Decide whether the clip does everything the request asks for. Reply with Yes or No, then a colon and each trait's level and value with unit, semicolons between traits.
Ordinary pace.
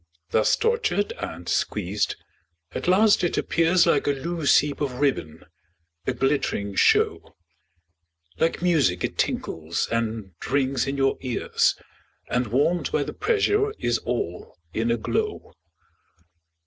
No: slow, 130 wpm